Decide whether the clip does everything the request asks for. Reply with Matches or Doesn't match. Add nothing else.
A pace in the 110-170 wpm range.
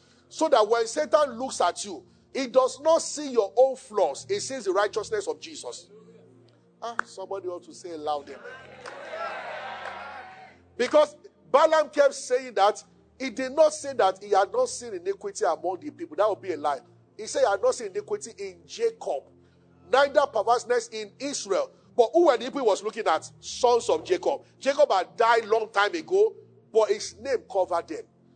Doesn't match